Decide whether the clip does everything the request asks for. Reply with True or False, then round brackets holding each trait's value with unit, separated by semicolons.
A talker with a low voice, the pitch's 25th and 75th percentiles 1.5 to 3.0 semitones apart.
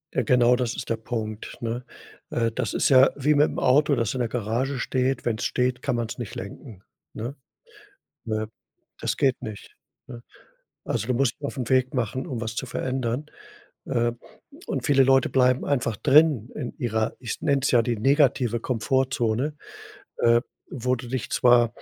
True (125 Hz; 2.4 semitones)